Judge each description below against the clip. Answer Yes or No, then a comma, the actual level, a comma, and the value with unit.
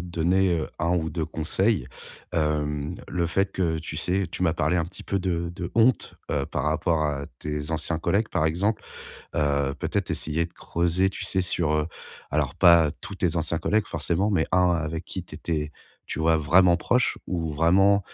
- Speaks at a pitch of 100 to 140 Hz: No, very low, 85 Hz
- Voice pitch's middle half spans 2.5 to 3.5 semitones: Yes, average, 2.9 semitones